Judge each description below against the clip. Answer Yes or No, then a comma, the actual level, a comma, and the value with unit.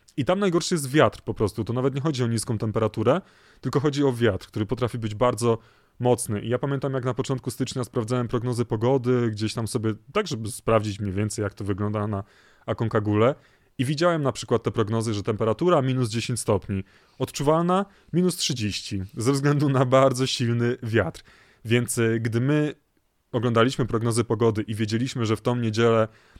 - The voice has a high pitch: No, low, 120 Hz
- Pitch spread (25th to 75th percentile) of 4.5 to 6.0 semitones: No, average, 3.2 semitones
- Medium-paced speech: No, fast, 175 wpm